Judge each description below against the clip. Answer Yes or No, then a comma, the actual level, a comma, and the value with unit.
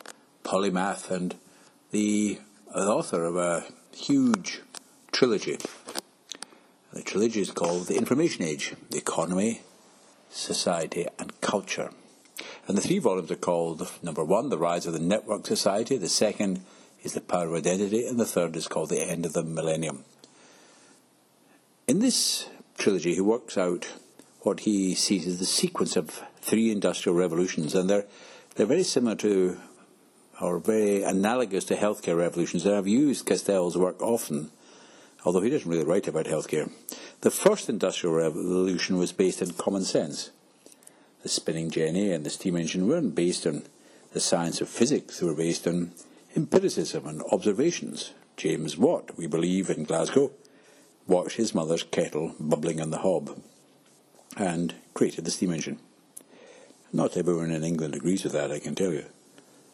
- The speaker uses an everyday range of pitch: Yes, average, 3.2 semitones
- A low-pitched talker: Yes, very low, 90 Hz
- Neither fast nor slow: Yes, average, 155 wpm